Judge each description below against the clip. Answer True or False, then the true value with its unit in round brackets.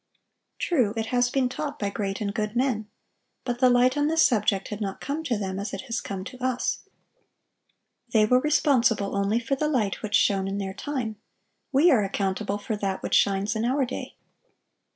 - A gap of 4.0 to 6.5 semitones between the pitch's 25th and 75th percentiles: True (4.3 semitones)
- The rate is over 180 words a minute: True (195 wpm)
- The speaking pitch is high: True (225 Hz)